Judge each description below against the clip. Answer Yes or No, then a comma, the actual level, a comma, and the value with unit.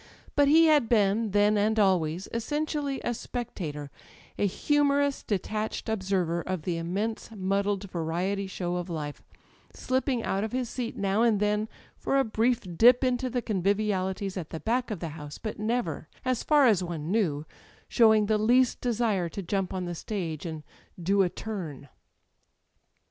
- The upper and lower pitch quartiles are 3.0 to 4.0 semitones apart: No, average, 4.8 semitones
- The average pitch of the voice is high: Yes, high, 205 Hz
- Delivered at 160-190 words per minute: Yes, average, 165 wpm